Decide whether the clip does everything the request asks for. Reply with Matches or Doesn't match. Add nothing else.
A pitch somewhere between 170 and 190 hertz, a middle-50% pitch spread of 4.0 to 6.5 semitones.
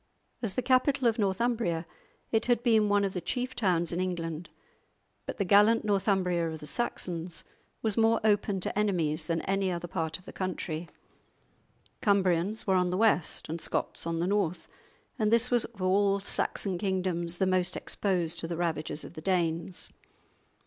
Doesn't match